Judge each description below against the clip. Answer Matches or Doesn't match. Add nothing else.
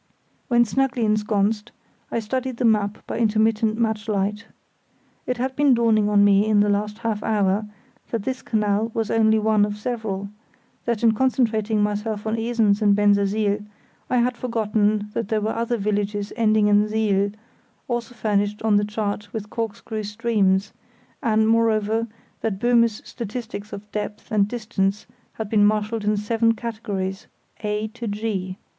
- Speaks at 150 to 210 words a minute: Matches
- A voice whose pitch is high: Matches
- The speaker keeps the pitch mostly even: Matches